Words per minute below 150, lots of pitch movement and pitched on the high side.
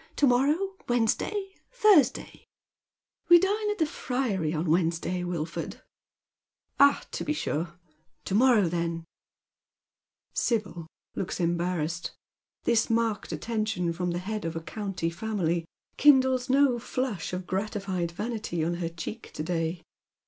Yes: average, 140 wpm; wide, 6.5 semitones; high, 195 Hz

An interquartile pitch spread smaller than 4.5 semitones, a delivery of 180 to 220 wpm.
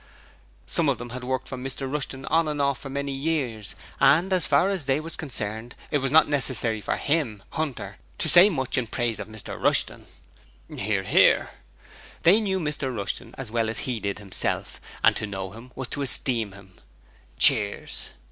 No: average, 5.0 semitones; average, 185 wpm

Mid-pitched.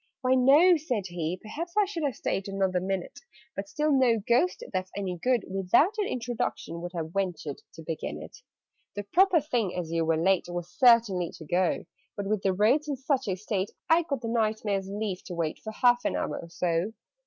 No: high, 205 Hz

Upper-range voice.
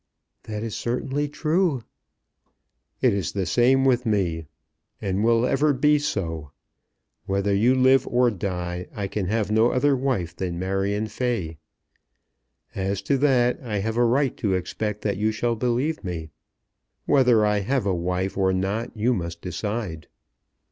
No: low, 110 Hz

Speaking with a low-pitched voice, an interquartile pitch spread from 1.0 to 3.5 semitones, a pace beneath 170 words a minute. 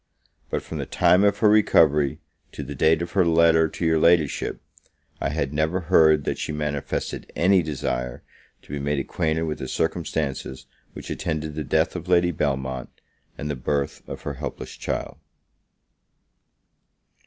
Yes: very low, 75 Hz; average, 2.8 semitones; average, 160 wpm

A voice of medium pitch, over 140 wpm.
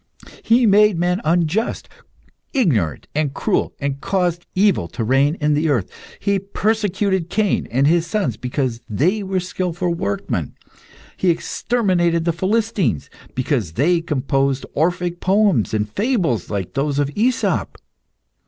No: medium, 170 Hz; slow, 135 wpm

